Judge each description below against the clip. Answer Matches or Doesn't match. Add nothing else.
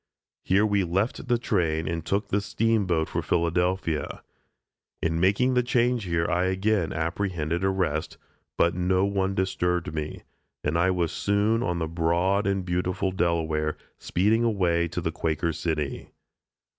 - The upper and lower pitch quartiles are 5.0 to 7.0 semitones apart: Doesn't match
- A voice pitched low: Matches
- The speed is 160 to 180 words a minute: Doesn't match